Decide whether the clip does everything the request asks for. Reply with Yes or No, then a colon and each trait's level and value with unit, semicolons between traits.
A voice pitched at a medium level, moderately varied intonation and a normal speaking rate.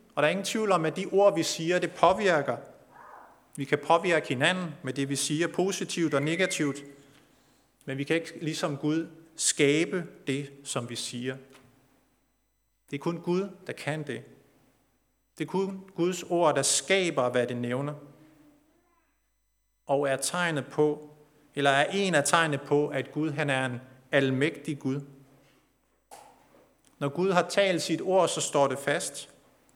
Yes: medium, 150 Hz; average, 3.9 semitones; average, 160 wpm